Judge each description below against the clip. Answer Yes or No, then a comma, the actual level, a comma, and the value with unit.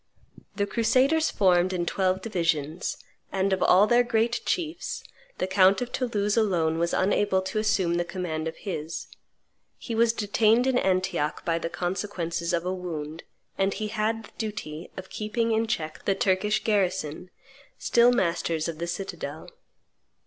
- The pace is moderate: Yes, average, 155 wpm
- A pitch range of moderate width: Yes, average, 4.3 semitones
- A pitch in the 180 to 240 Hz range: Yes, high, 190 Hz